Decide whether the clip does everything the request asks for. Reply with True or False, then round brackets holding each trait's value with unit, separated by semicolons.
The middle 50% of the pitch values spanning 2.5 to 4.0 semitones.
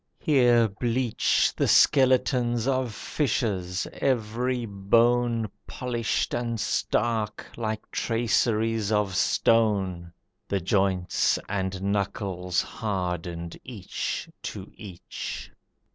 True (3.7 semitones)